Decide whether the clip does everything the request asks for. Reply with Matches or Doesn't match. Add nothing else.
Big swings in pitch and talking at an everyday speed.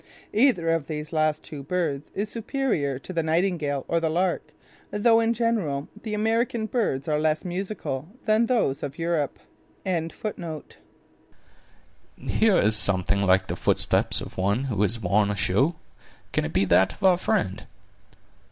Matches